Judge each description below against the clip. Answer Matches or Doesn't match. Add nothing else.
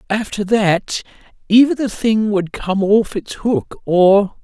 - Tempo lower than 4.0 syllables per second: Matches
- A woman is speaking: Doesn't match